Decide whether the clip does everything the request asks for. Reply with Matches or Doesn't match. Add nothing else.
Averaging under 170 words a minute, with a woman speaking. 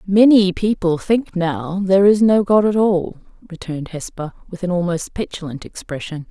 Matches